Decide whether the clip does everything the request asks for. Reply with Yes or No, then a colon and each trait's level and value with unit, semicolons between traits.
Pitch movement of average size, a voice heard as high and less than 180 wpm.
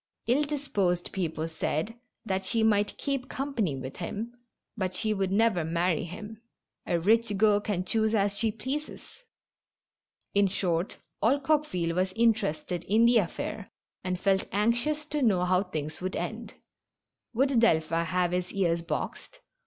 Yes: average, 4.4 semitones; high, 200 Hz; average, 155 wpm